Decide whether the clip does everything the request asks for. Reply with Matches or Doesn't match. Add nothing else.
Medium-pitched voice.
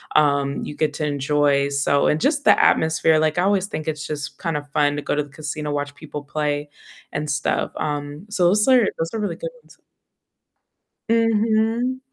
Matches